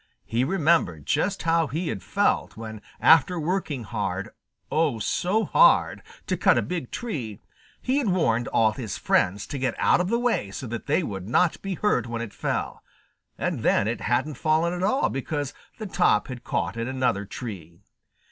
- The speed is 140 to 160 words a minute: No, average, 185 wpm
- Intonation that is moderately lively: No, wide, 8.0 semitones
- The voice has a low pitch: Yes, low, 130 Hz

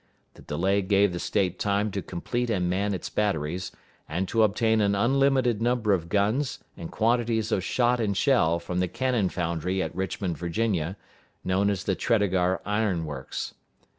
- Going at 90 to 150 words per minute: No, average, 165 wpm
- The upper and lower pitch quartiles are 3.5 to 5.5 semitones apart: Yes, average, 3.9 semitones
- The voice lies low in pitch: Yes, low, 100 Hz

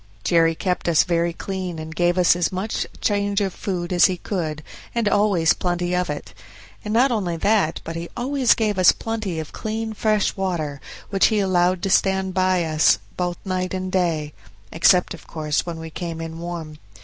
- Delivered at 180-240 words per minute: Yes, average, 190 wpm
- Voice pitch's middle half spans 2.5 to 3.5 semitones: Yes, average, 3.0 semitones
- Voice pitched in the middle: Yes, medium, 180 Hz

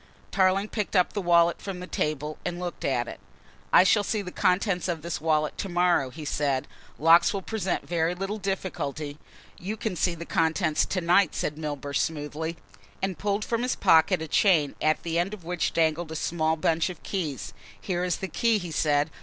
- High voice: No, medium, 170 Hz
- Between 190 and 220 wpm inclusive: Yes, fast, 205 wpm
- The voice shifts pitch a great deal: No, average, 3.4 semitones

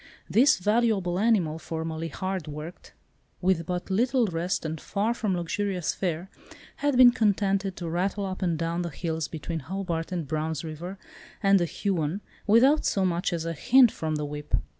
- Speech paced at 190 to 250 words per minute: No, average, 170 wpm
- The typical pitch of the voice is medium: Yes, medium, 180 Hz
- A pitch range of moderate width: Yes, average, 3.7 semitones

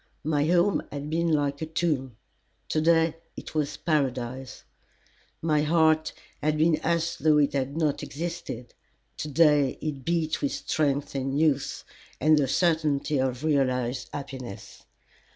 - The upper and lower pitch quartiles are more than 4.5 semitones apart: No, average, 2.7 semitones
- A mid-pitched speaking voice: Yes, medium, 150 Hz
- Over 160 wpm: No, average, 140 wpm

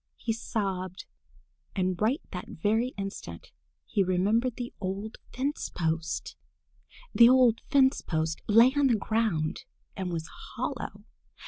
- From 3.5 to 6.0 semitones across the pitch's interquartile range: Yes, average, 4.6 semitones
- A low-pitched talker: No, high, 210 Hz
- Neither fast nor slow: No, slow, 125 wpm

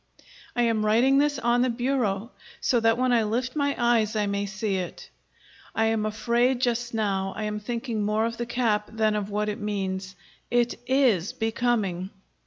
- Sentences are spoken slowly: No, average, 185 wpm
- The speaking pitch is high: Yes, high, 225 Hz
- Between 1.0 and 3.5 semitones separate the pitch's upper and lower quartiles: Yes, narrow, 2.5 semitones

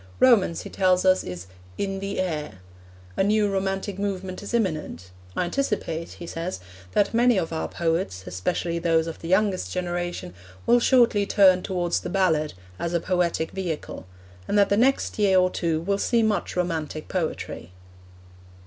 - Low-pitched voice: No, medium, 185 Hz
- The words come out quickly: No, average, 165 wpm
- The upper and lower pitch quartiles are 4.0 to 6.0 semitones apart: No, average, 3.3 semitones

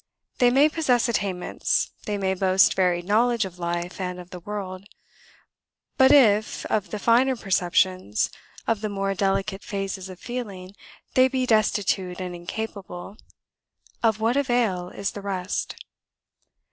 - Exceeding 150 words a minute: No, average, 140 wpm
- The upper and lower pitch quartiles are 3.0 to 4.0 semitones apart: Yes, average, 3.7 semitones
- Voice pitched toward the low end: No, high, 200 Hz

